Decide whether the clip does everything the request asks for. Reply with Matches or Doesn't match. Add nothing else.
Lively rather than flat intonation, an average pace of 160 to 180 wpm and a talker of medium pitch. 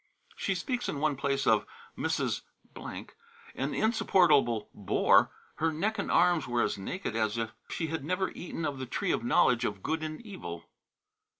Matches